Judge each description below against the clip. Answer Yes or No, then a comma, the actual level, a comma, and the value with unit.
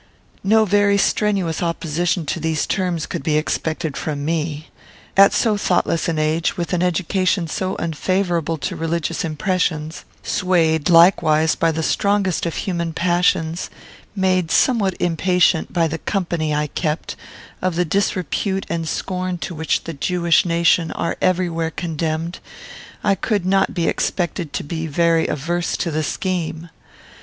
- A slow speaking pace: No, average, 145 wpm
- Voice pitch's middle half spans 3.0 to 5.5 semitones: No, narrow, 2.4 semitones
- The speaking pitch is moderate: Yes, medium, 170 Hz